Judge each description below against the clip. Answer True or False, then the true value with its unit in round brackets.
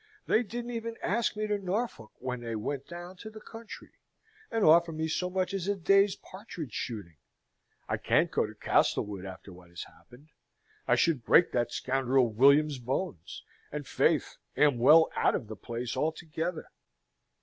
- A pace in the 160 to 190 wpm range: True (170 wpm)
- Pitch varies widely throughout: True (8.0 semitones)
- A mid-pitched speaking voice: True (155 Hz)